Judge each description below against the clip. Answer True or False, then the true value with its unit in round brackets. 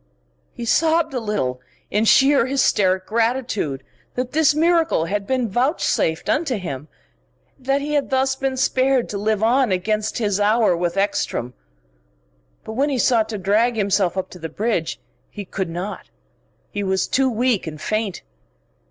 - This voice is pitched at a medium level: False (220 Hz)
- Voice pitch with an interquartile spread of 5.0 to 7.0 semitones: True (5.5 semitones)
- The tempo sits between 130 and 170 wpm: True (160 wpm)